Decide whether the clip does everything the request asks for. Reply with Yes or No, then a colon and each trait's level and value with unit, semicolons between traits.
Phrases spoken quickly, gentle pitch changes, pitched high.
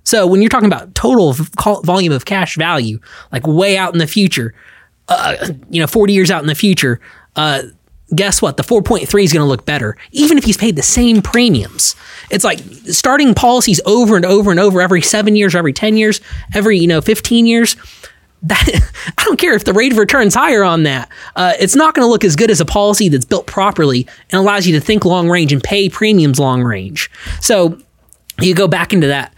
No: fast, 225 wpm; average, 5.3 semitones; high, 195 Hz